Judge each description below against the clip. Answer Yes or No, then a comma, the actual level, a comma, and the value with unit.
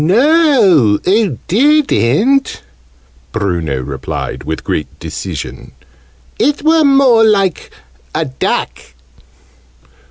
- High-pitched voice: Yes, high, 195 Hz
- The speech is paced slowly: Yes, slow, 85 wpm